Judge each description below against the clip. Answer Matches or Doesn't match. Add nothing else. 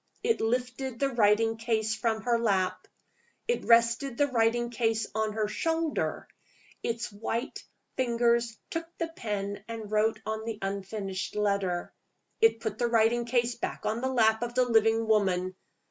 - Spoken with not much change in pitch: Matches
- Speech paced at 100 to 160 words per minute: Matches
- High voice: Matches